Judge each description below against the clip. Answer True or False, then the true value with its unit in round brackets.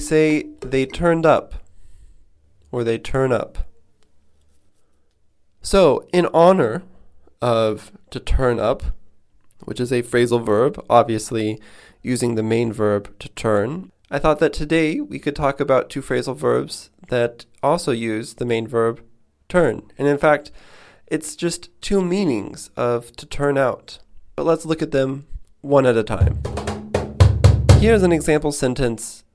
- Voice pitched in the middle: False (120 Hz)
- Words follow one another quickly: False (140 wpm)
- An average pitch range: False (6.0 semitones)